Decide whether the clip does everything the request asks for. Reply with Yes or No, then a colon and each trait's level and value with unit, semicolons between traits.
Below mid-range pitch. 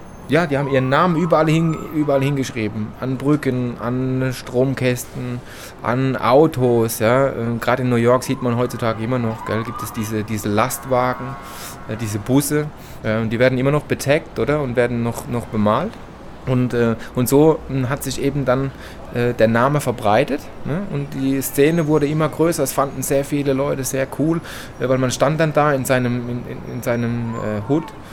Yes: low, 130 Hz